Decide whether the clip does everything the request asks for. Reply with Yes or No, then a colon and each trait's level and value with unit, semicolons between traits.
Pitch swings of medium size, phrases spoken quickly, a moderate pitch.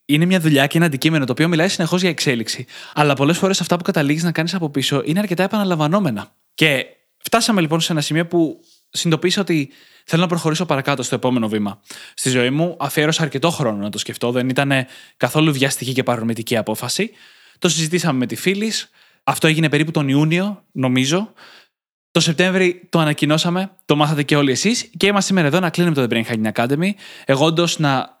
Yes: average, 4.7 semitones; fast, 190 wpm; medium, 155 Hz